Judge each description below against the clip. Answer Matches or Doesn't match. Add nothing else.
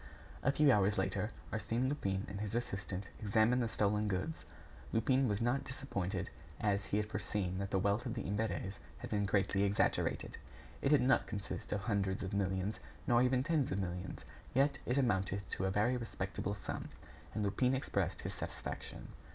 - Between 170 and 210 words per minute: Matches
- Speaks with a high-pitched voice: Doesn't match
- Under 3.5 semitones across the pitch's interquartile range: Doesn't match